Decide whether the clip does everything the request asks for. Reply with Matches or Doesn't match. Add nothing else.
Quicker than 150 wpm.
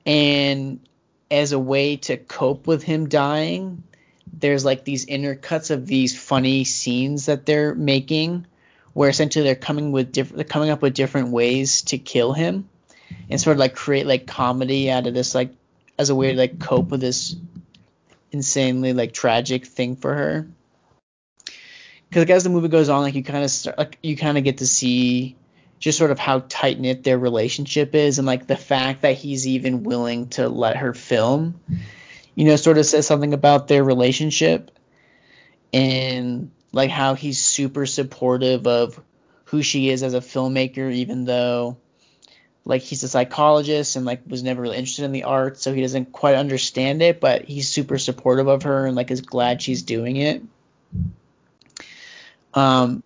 Matches